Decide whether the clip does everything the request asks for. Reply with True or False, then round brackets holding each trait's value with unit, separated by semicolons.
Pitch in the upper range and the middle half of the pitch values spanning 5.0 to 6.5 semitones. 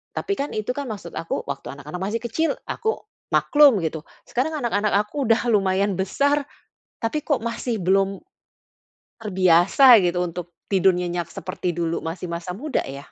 True (195 Hz; 5.4 semitones)